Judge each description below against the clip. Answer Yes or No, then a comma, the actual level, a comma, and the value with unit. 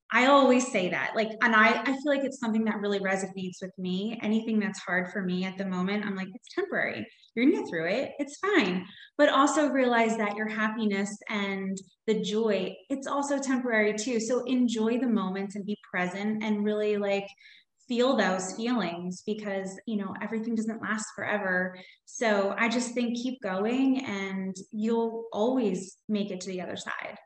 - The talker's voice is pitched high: Yes, high, 215 Hz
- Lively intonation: No, average, 3.8 semitones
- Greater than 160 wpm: Yes, average, 185 wpm